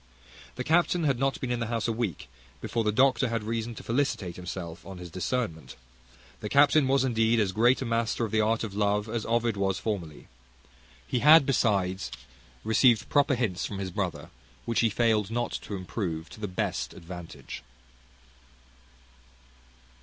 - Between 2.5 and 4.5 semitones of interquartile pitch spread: Yes, average, 3.9 semitones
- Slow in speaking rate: No, average, 170 wpm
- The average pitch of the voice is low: Yes, low, 110 Hz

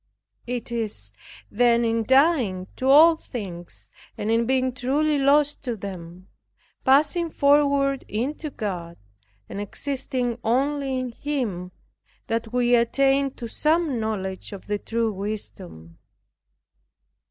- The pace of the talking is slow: Yes, slow, 120 wpm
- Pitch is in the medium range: No, high, 245 Hz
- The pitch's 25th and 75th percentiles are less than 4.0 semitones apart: No, average, 5.0 semitones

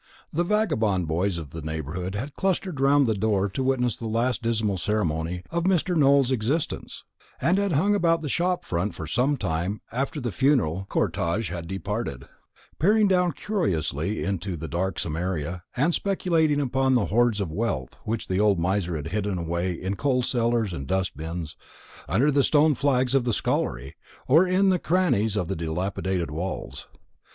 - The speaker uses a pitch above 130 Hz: No, low, 110 Hz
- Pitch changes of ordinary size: No, wide, 8.2 semitones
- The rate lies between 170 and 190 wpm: Yes, average, 175 wpm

